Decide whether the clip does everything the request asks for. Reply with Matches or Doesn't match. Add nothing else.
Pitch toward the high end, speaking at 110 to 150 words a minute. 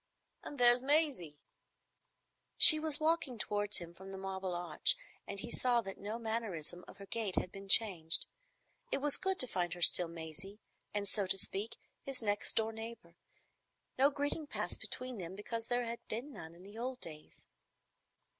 Doesn't match